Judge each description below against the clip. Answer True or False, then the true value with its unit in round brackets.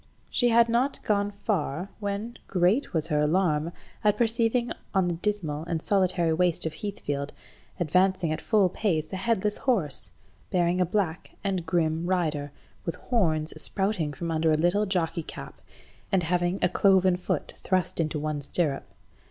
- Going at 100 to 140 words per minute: False (155 wpm)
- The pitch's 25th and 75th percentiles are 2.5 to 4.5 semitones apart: True (4.0 semitones)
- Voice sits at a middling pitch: True (180 Hz)